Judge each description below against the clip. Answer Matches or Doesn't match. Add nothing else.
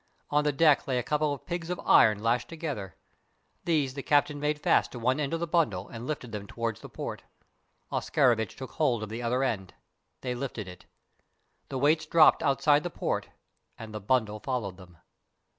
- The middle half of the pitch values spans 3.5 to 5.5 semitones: Matches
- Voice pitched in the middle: Doesn't match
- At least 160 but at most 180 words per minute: Doesn't match